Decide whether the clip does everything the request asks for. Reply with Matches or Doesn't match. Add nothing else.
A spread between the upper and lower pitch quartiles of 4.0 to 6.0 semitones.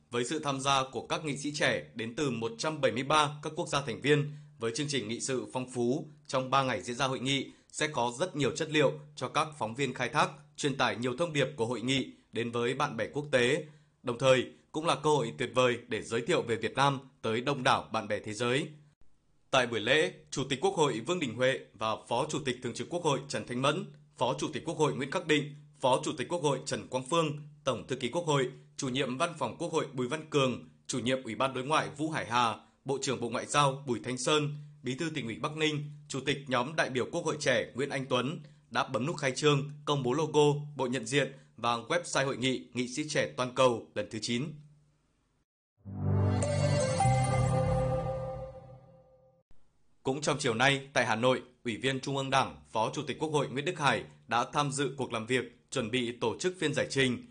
Doesn't match